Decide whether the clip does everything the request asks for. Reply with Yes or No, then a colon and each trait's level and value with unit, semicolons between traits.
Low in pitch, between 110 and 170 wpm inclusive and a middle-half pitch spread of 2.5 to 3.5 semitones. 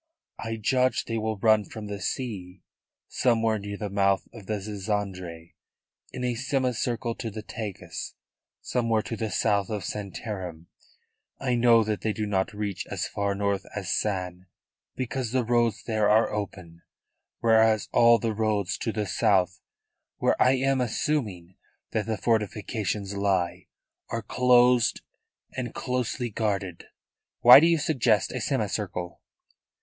Yes: low, 110 Hz; average, 140 wpm; average, 3.0 semitones